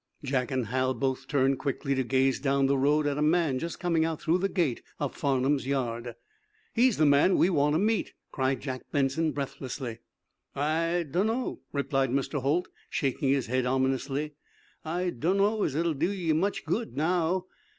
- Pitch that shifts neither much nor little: Yes, average, 3.9 semitones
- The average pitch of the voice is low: No, medium, 145 Hz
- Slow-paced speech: No, average, 175 wpm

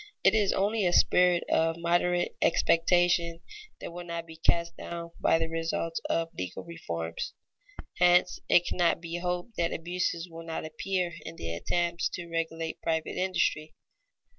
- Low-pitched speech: No, medium, 170 Hz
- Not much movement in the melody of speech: Yes, narrow, 1.3 semitones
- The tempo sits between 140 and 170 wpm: Yes, average, 155 wpm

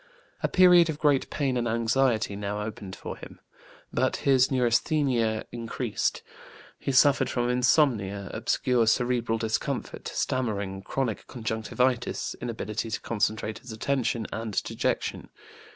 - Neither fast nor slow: No, slow, 120 wpm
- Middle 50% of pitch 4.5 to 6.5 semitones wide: No, average, 3.1 semitones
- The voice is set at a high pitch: No, low, 120 Hz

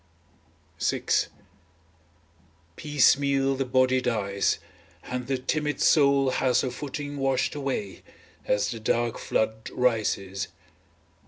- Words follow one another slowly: Yes, slow, 100 wpm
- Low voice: Yes, low, 130 Hz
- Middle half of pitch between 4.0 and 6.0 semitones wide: No, average, 3.4 semitones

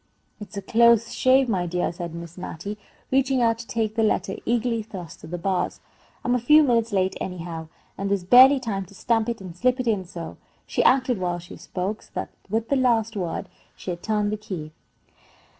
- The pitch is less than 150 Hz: No, high, 210 Hz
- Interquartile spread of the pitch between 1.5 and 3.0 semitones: No, average, 4.6 semitones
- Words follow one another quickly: Yes, fast, 210 wpm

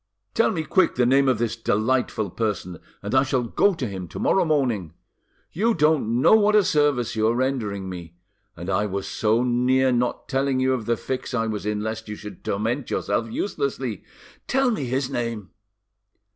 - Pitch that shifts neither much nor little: Yes, average, 4.3 semitones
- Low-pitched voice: Yes, low, 120 Hz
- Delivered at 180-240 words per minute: Yes, average, 190 wpm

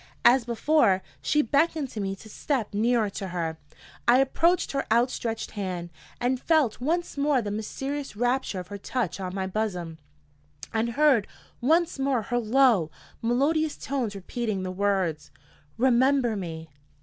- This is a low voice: No, high, 235 Hz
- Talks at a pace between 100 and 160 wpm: Yes, average, 150 wpm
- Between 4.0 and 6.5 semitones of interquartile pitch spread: Yes, wide, 5.6 semitones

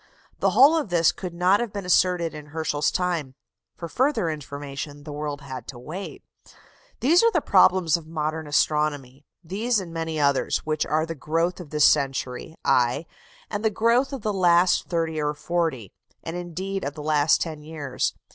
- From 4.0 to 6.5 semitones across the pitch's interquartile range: No, average, 3.6 semitones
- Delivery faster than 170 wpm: Yes, average, 180 wpm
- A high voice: No, medium, 160 Hz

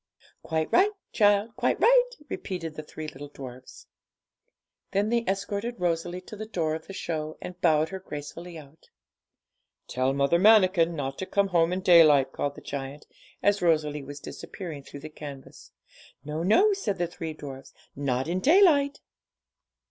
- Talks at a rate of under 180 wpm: Yes, average, 160 wpm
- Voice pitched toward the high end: No, medium, 165 Hz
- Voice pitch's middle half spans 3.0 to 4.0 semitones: No, average, 5.2 semitones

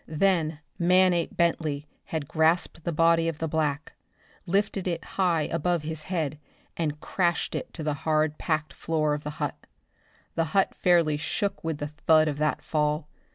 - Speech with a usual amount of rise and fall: No, narrow, 2.1 semitones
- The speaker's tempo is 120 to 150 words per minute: No, average, 165 wpm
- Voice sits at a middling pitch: Yes, medium, 160 Hz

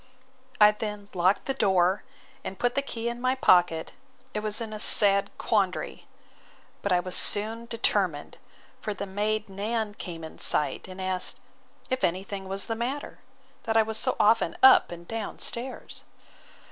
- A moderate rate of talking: Yes, average, 170 wpm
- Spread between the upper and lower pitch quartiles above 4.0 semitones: No, average, 3.2 semitones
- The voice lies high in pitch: Yes, high, 210 Hz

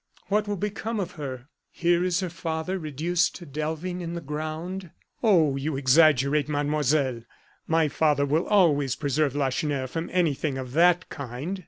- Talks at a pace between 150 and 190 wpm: Yes, average, 155 wpm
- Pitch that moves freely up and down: No, average, 3.7 semitones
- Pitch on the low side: No, medium, 155 Hz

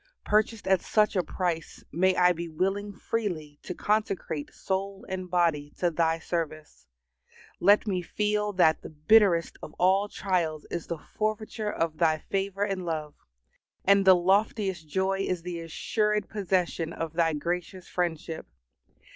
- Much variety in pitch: No, average, 3.3 semitones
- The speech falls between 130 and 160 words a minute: Yes, average, 145 wpm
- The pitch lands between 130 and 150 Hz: No, medium, 180 Hz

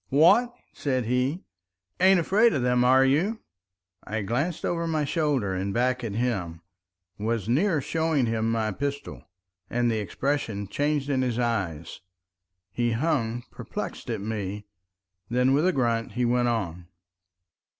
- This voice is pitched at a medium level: No, low, 125 Hz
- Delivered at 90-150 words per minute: Yes, average, 145 wpm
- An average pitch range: Yes, average, 4.7 semitones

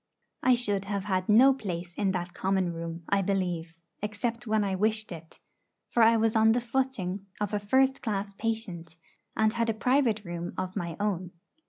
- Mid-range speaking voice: No, high, 205 Hz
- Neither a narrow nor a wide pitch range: Yes, average, 3.7 semitones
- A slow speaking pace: No, average, 185 wpm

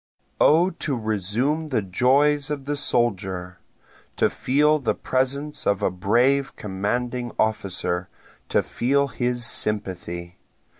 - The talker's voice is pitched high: No, low, 120 Hz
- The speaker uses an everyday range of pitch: No, wide, 6.0 semitones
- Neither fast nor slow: No, slow, 115 wpm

